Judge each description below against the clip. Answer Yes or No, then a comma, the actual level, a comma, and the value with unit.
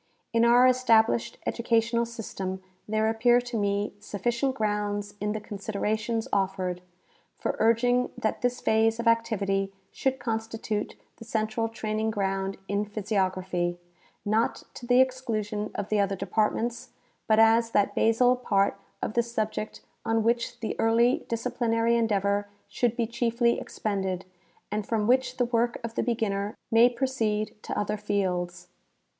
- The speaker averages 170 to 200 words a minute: No, average, 145 wpm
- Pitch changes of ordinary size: No, narrow, 2.3 semitones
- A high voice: Yes, high, 220 Hz